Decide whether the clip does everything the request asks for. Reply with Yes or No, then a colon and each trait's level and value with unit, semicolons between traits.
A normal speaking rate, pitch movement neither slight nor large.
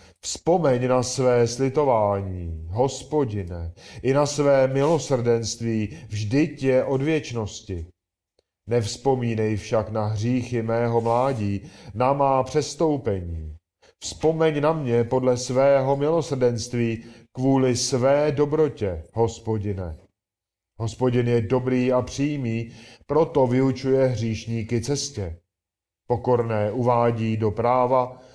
No: slow, 95 wpm; average, 3.6 semitones